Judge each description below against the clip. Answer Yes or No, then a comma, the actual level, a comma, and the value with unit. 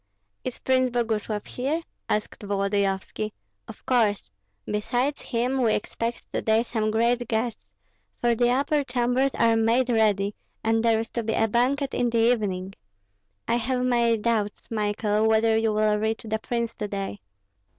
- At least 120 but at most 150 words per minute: No, average, 160 wpm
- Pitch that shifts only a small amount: Yes, narrow, 2.3 semitones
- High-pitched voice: Yes, high, 225 Hz